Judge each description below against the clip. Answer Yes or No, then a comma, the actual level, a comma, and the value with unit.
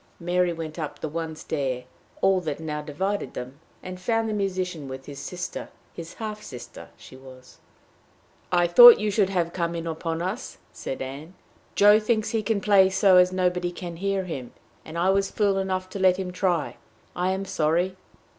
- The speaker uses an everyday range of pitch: Yes, average, 3.3 semitones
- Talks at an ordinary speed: Yes, average, 185 wpm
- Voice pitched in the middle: Yes, medium, 180 Hz